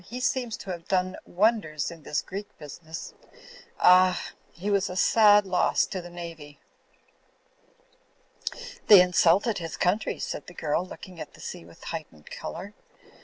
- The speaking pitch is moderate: Yes, medium, 180 Hz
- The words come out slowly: No, average, 155 wpm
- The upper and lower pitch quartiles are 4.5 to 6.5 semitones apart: No, average, 3.4 semitones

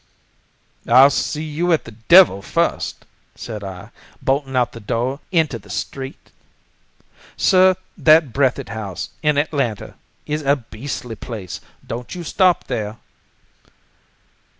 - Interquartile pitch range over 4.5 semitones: Yes, average, 5.1 semitones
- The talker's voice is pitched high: No, low, 135 Hz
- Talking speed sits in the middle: No, slow, 125 wpm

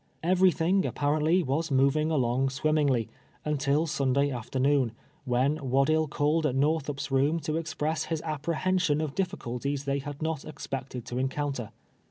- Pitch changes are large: No, average, 2.7 semitones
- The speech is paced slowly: No, average, 145 wpm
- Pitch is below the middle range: No, medium, 145 Hz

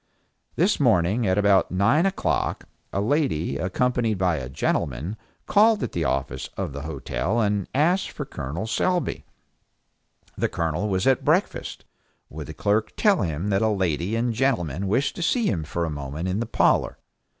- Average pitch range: No, wide, 6.9 semitones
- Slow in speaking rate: No, average, 170 wpm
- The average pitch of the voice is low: Yes, very low, 95 Hz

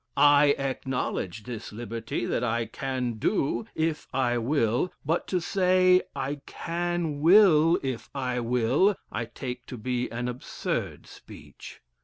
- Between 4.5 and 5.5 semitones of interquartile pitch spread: Yes, average, 5.1 semitones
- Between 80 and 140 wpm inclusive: Yes, slow, 135 wpm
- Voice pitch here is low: Yes, low, 130 Hz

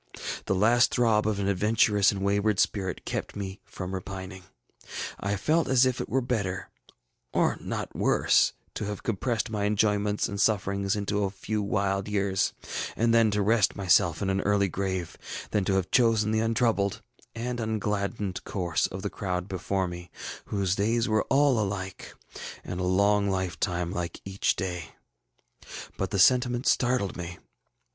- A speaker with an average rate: Yes, average, 160 wpm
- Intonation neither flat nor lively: No, narrow, 2.3 semitones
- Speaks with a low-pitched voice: Yes, low, 100 Hz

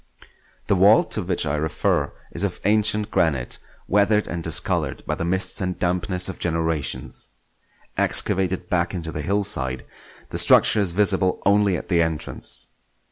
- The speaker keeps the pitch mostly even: No, average, 3.5 semitones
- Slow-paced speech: No, average, 150 wpm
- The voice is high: No, very low, 90 Hz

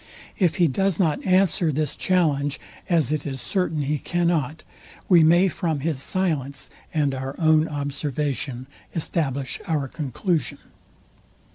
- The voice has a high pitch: No, medium, 155 Hz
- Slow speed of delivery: Yes, slow, 130 wpm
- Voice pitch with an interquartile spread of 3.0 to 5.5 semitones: Yes, average, 3.5 semitones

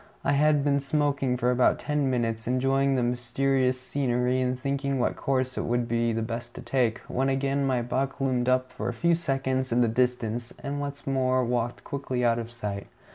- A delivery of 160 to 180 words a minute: No, average, 195 wpm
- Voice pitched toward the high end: No, low, 130 Hz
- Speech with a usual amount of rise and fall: No, narrow, 2.2 semitones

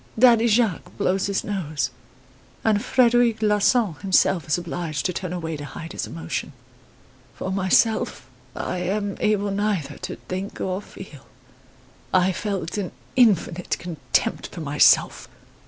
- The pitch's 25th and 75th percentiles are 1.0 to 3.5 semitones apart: No, average, 4.1 semitones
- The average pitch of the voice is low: No, high, 190 Hz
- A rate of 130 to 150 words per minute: Yes, slow, 135 wpm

